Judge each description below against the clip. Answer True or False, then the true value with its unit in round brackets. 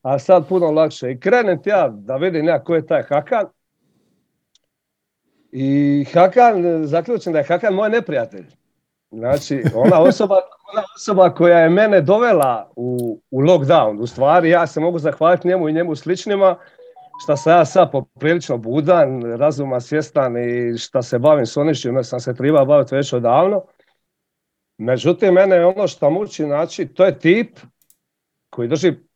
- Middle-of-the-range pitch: True (165 Hz)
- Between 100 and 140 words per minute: False (160 wpm)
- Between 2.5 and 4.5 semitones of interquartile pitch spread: False (5.1 semitones)